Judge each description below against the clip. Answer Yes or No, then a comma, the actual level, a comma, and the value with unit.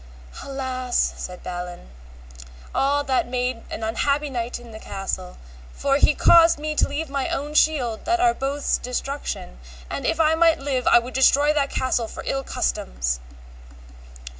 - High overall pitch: Yes, very high, 270 Hz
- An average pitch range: Yes, average, 3.8 semitones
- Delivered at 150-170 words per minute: Yes, average, 160 wpm